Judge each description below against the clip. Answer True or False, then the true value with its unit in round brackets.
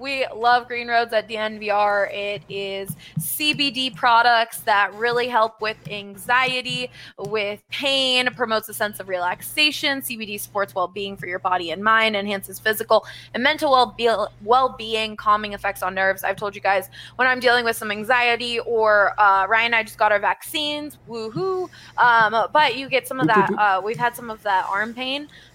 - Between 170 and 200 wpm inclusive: True (175 wpm)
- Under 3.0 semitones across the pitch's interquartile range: False (3.5 semitones)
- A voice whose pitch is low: False (220 Hz)